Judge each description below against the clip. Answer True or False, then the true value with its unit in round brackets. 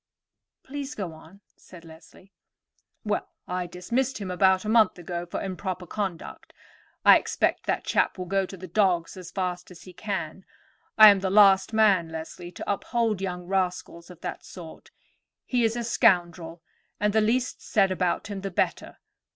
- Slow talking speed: False (165 wpm)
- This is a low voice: False (190 Hz)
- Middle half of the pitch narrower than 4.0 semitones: True (2.9 semitones)